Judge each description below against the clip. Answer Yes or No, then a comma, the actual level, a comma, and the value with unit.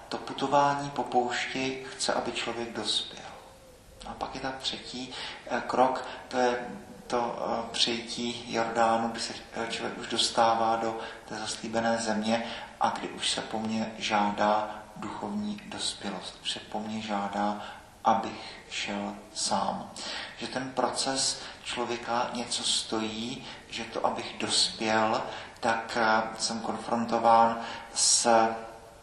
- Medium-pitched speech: No, low, 115 Hz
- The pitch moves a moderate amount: No, narrow, 1.7 semitones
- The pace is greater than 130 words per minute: No, average, 120 wpm